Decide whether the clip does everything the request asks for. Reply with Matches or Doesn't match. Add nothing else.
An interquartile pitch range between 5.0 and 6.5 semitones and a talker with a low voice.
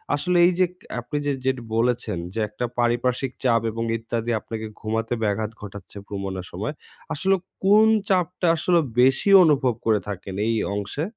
Matches